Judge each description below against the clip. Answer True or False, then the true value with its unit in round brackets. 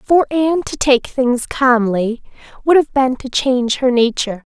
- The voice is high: True (260 Hz)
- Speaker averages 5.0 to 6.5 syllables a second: False (4.6 syllables/s)